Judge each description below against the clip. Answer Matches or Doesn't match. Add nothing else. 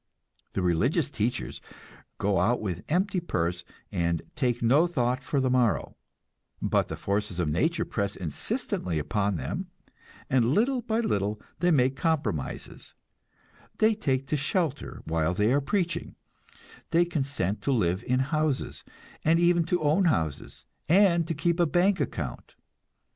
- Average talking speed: Matches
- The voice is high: Doesn't match